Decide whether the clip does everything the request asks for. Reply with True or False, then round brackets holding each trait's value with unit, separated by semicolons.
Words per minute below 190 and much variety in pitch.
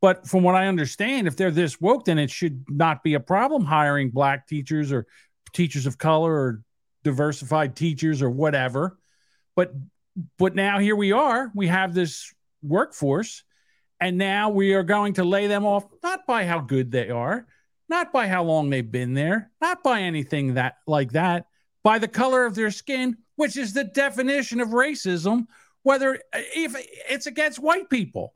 True (180 wpm; 7.9 semitones)